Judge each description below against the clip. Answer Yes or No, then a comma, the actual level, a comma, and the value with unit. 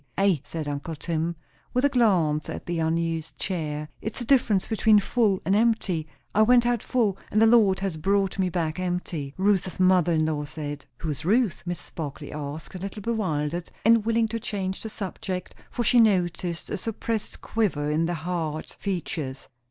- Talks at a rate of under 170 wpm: No, average, 185 wpm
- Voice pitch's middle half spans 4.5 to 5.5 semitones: Yes, average, 5.1 semitones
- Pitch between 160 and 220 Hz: Yes, medium, 185 Hz